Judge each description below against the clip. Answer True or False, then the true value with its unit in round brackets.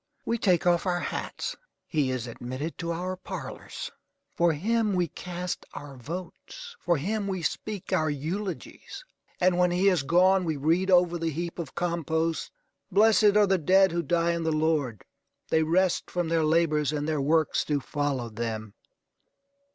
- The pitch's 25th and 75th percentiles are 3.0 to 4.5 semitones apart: True (3.3 semitones)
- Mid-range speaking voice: True (170 Hz)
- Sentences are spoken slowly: False (165 wpm)